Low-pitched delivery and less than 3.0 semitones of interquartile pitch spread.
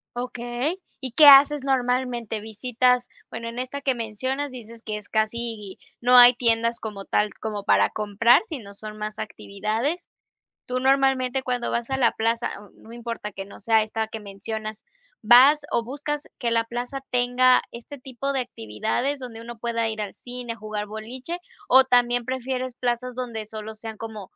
No: high, 235 Hz; narrow, 2.6 semitones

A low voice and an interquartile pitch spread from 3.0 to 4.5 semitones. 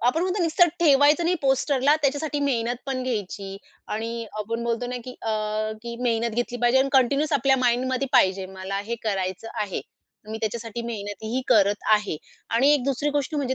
No: high, 240 Hz; average, 4.0 semitones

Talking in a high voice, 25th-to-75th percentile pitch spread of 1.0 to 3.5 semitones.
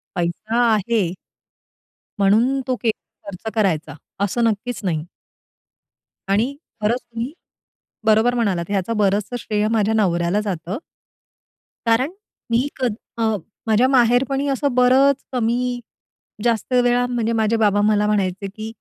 Yes: high, 225 Hz; average, 3.2 semitones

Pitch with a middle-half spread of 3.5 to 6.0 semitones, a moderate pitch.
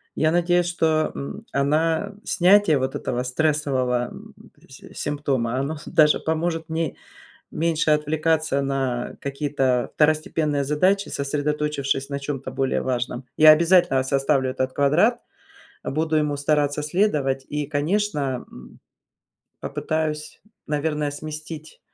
No: narrow, 2.6 semitones; medium, 150 Hz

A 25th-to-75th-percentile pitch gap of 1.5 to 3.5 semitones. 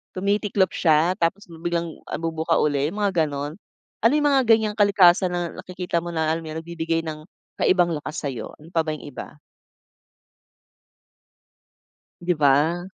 Yes: average, 2.8 semitones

